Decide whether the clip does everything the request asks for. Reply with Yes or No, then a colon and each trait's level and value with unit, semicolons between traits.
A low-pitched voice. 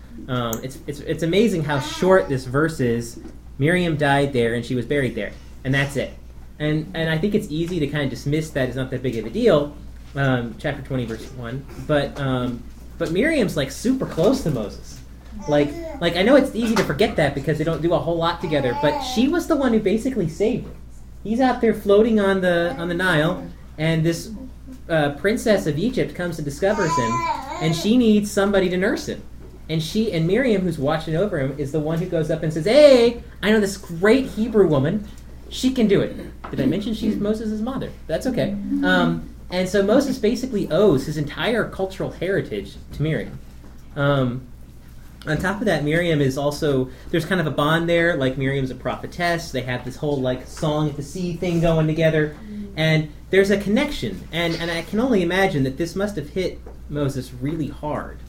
No: medium, 160 Hz